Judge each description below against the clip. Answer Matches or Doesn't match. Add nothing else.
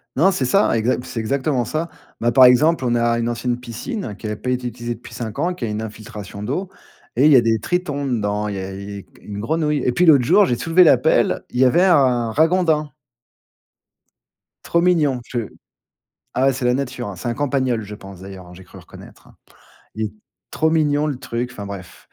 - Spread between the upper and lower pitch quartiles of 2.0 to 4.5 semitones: Doesn't match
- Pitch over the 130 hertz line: Doesn't match